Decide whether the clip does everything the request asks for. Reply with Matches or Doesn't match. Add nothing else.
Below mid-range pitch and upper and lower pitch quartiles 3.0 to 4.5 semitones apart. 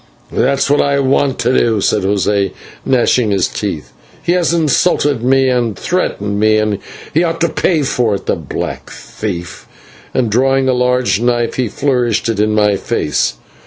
Matches